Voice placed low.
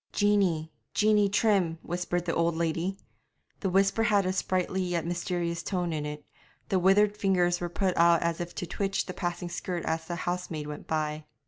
No: medium, 175 Hz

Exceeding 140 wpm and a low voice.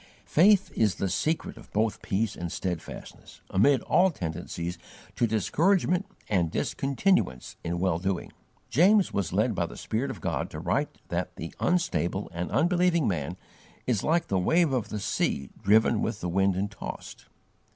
Yes: average, 160 wpm; low, 105 Hz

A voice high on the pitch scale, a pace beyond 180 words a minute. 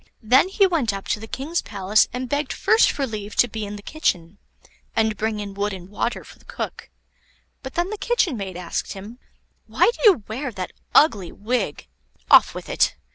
Yes: high, 220 Hz; average, 200 wpm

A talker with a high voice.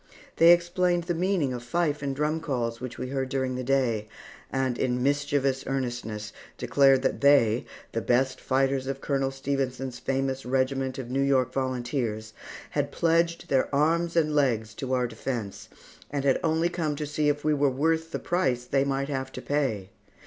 No: low, 135 Hz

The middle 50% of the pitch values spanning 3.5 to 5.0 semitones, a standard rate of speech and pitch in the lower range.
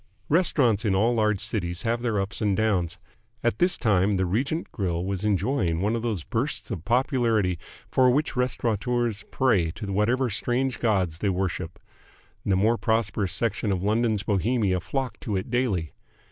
Yes: average, 4.1 semitones; average, 165 wpm; low, 110 Hz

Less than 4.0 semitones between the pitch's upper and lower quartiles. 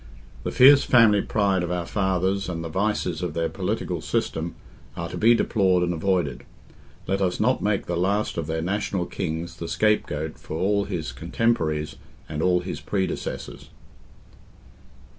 Yes: average, 3.4 semitones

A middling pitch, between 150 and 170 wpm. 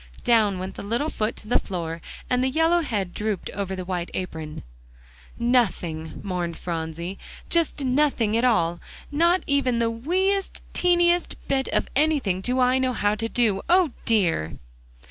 No: high, 230 Hz; average, 165 wpm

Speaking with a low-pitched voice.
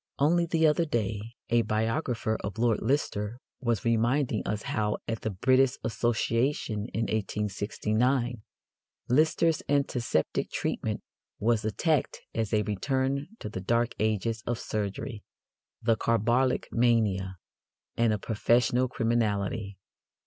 Yes: low, 115 Hz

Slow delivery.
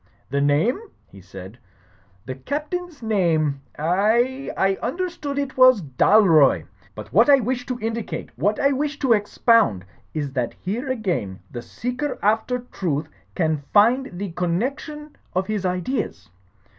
No: average, 145 wpm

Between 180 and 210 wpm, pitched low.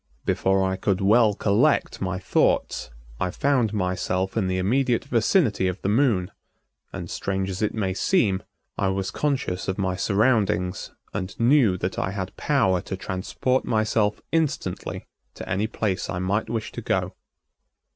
No: average, 155 wpm; low, 100 Hz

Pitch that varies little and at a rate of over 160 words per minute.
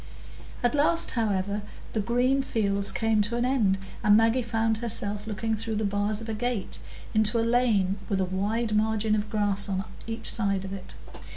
Yes: narrow, 2.2 semitones; average, 185 wpm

